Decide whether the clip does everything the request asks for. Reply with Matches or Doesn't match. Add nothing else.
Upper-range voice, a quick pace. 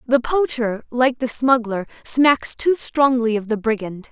Doesn't match